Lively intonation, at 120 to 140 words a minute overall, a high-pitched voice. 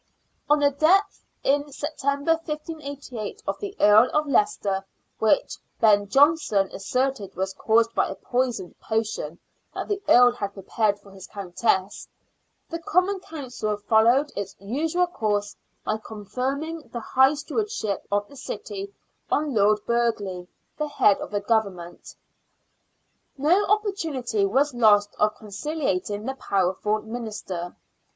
Yes: wide, 6.5 semitones; slow, 135 wpm; high, 235 Hz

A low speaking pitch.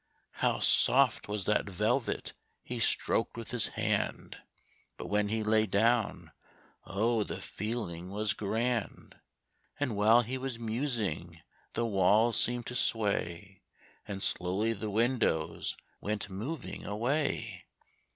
Yes: low, 110 Hz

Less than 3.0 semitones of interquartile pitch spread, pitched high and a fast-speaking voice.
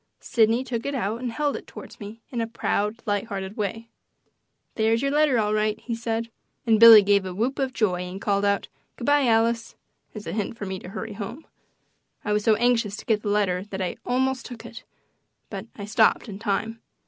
Yes: narrow, 2.5 semitones; high, 225 Hz; fast, 215 wpm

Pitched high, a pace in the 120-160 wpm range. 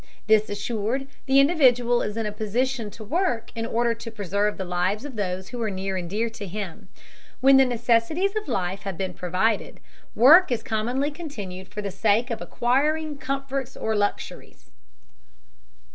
No: high, 225 Hz; average, 170 wpm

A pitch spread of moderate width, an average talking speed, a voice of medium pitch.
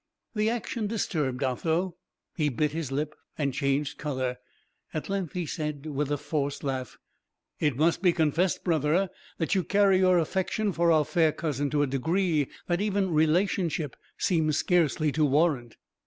Yes: average, 3.7 semitones; average, 160 wpm; medium, 155 Hz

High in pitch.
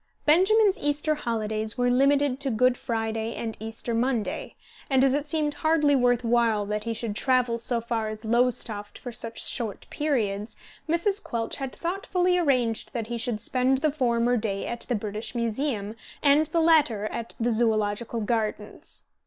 Yes: high, 240 Hz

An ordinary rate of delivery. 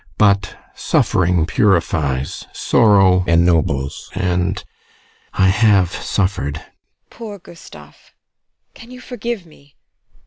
No: slow, 95 wpm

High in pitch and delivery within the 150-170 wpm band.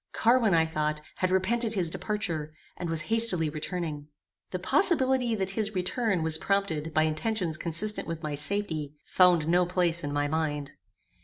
No: medium, 175 Hz; average, 160 wpm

